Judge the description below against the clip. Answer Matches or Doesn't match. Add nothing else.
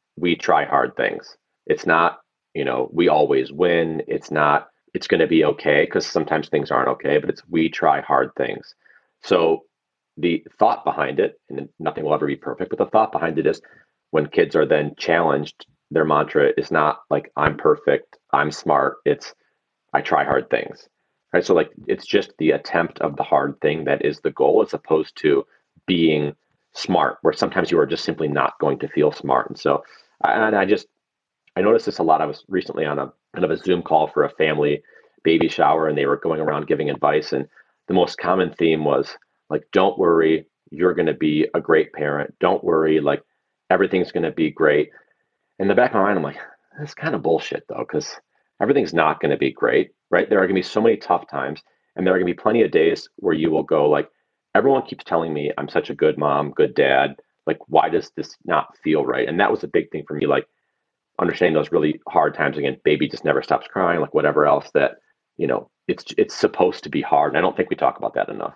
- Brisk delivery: Matches